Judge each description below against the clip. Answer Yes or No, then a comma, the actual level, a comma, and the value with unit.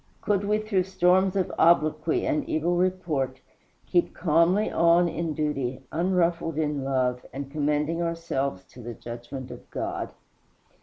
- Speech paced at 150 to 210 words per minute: No, average, 140 wpm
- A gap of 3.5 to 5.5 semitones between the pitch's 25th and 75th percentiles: Yes, average, 4.3 semitones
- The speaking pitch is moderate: Yes, medium, 160 Hz